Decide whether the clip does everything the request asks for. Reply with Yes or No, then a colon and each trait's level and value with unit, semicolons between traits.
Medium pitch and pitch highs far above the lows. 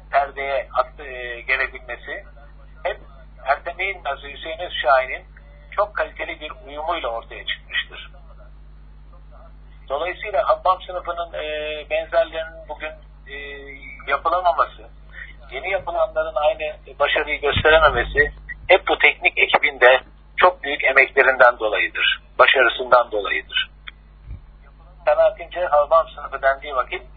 Yes: medium, 160 Hz; wide, 7.2 semitones